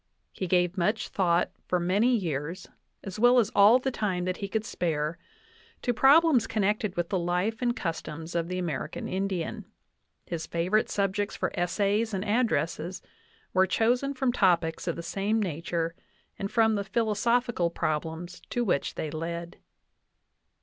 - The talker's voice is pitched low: No, high, 190 Hz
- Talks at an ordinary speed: Yes, average, 155 wpm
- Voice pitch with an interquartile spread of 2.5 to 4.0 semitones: No, average, 4.5 semitones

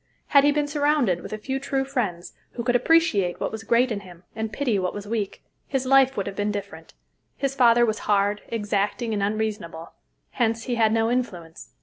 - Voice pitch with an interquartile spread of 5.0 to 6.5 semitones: No, average, 4.3 semitones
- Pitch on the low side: No, high, 225 Hz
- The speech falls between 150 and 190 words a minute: No, fast, 205 wpm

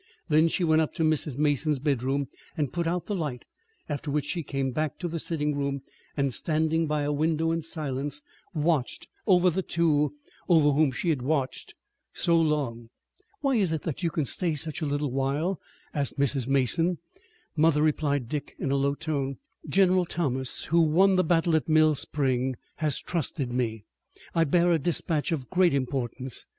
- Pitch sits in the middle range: Yes, medium, 150 Hz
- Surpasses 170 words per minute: Yes, average, 180 wpm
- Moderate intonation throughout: Yes, average, 3.0 semitones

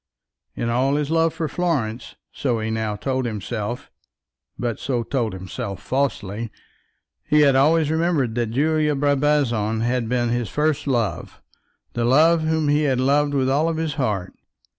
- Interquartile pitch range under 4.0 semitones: No, average, 4.3 semitones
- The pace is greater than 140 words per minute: Yes, average, 155 wpm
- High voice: No, low, 130 Hz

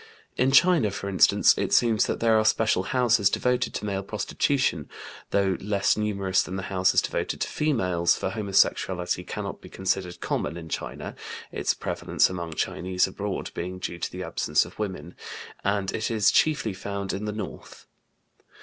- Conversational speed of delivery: Yes, average, 165 wpm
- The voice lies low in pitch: Yes, low, 100 Hz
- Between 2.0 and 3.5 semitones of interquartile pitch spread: Yes, average, 2.8 semitones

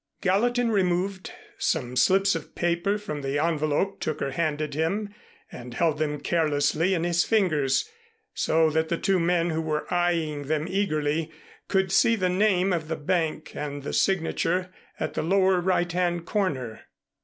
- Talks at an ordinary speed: Yes, average, 155 wpm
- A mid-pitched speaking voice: Yes, medium, 170 Hz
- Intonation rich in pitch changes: No, average, 3.6 semitones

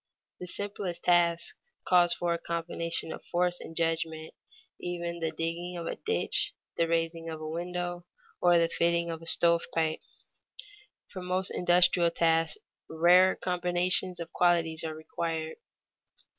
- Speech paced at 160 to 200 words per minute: No, average, 145 wpm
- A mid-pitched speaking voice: Yes, medium, 170 Hz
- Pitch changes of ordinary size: No, narrow, 1.2 semitones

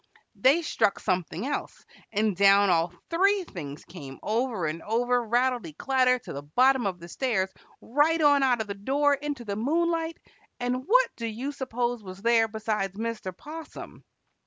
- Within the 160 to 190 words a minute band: Yes, average, 165 wpm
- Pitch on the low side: No, high, 235 Hz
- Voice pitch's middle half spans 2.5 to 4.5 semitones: No, wide, 5.6 semitones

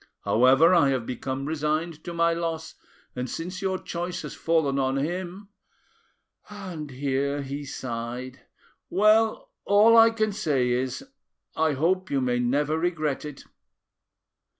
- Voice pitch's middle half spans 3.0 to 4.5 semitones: No, average, 5.3 semitones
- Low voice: No, medium, 155 Hz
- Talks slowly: Yes, slow, 125 wpm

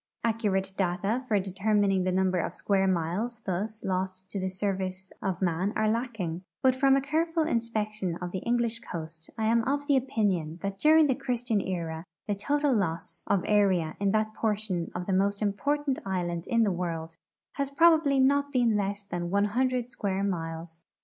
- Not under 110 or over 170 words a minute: No, average, 180 wpm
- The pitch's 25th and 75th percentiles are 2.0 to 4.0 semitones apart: No, average, 4.5 semitones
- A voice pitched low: No, high, 200 Hz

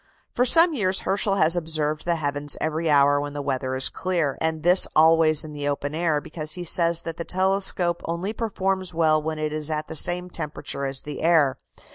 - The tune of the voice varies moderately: Yes, average, 3.2 semitones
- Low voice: No, medium, 160 Hz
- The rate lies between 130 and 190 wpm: No, fast, 205 wpm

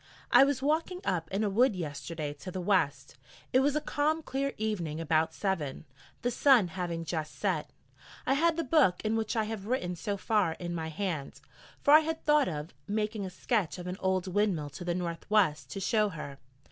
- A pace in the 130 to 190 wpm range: No, fast, 205 wpm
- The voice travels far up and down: Yes, wide, 6.6 semitones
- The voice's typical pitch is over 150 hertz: Yes, high, 190 Hz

